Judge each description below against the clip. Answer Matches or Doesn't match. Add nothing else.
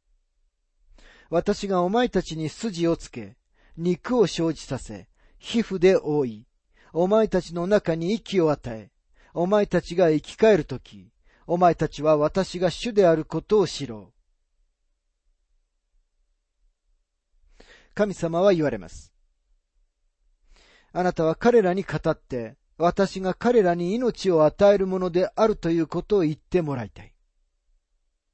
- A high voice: Doesn't match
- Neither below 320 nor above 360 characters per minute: Doesn't match